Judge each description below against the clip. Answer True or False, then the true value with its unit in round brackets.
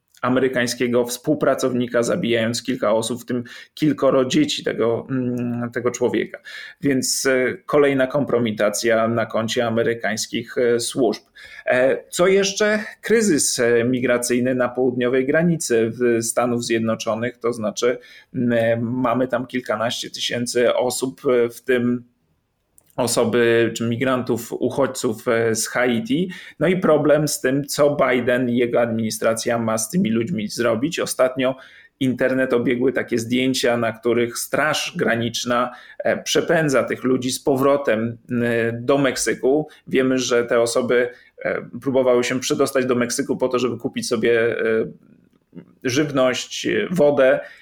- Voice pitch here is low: True (125 Hz)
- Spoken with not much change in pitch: True (1.9 semitones)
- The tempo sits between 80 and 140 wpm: True (115 wpm)